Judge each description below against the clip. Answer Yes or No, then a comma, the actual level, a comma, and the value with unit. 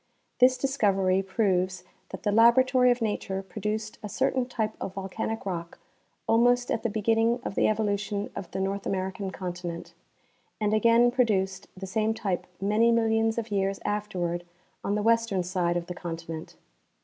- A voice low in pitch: No, high, 205 Hz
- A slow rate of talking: No, average, 160 wpm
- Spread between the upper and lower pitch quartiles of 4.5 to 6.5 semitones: No, average, 3.1 semitones